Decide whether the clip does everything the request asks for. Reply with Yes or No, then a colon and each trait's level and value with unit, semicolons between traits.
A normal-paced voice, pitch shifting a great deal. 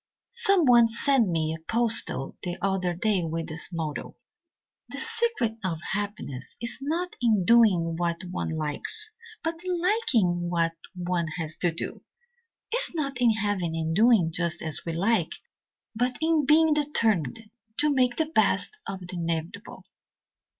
Yes: average, 150 wpm; wide, 8.5 semitones